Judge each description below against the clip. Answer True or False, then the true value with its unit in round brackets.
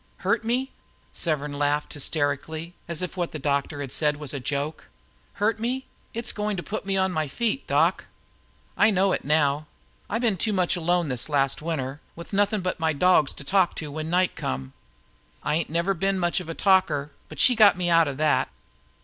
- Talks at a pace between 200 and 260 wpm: True (205 wpm)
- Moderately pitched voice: True (165 Hz)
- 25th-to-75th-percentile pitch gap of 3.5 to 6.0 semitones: True (4.8 semitones)